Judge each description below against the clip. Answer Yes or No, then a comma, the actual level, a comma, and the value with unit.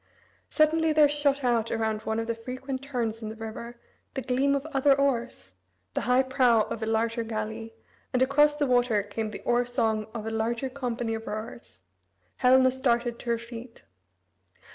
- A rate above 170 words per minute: Yes, average, 180 wpm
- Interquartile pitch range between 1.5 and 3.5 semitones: Yes, average, 2.7 semitones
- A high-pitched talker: Yes, high, 240 Hz